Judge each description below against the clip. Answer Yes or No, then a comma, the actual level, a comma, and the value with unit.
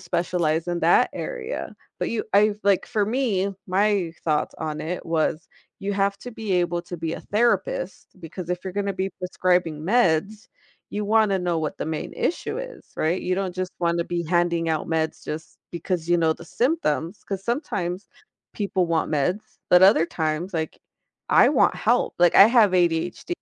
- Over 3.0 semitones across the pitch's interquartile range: Yes, average, 3.5 semitones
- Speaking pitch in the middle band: Yes, medium, 180 Hz